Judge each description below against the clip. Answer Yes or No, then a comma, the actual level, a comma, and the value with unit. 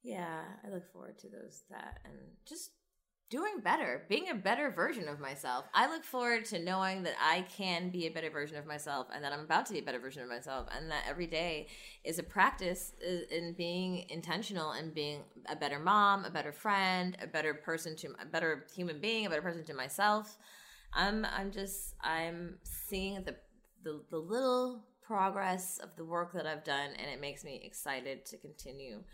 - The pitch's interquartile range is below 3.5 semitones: No, average, 4.1 semitones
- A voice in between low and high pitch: Yes, medium, 175 Hz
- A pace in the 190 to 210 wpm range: Yes, average, 200 wpm